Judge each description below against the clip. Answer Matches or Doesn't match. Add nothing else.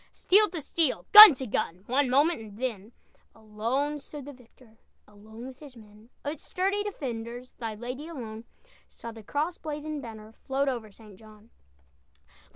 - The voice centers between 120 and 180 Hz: Doesn't match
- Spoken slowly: Doesn't match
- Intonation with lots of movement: Doesn't match